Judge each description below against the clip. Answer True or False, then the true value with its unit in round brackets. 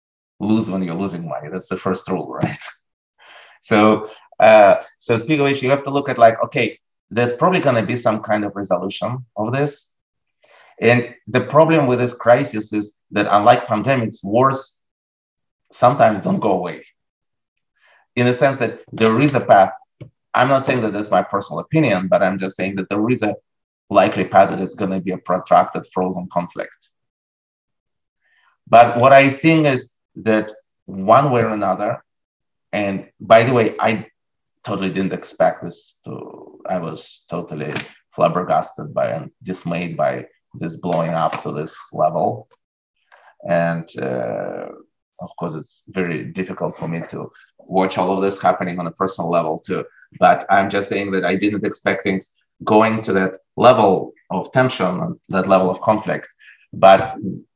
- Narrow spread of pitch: False (4.6 semitones)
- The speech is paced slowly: False (165 wpm)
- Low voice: True (105 Hz)